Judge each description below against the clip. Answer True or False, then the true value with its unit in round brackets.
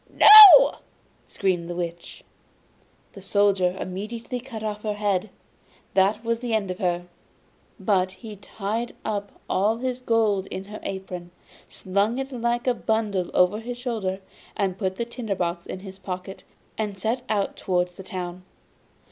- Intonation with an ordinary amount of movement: True (3.5 semitones)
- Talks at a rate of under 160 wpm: True (150 wpm)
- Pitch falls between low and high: False (200 Hz)